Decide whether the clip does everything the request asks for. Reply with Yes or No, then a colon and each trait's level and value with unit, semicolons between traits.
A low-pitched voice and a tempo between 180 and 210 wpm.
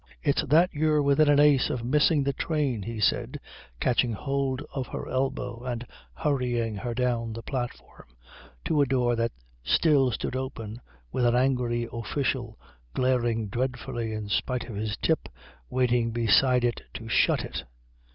No: low, 125 Hz; average, 155 wpm